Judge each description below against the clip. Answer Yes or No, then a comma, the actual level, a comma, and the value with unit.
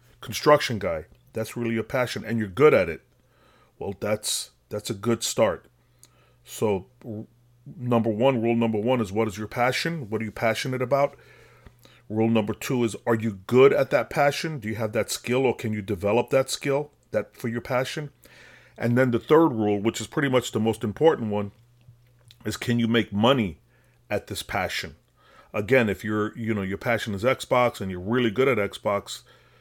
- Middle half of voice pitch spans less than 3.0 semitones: Yes, narrow, 2.5 semitones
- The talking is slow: No, average, 195 wpm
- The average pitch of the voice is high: No, low, 115 Hz